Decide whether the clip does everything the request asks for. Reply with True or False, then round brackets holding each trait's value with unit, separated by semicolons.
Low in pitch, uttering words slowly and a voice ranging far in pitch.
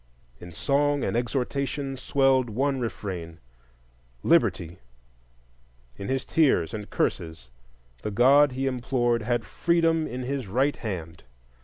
True (120 Hz; 115 wpm; 7.9 semitones)